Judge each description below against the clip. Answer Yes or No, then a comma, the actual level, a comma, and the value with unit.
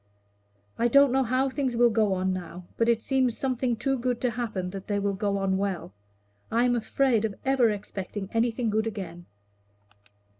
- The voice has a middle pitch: No, high, 225 Hz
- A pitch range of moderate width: Yes, average, 3.9 semitones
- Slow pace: No, average, 185 wpm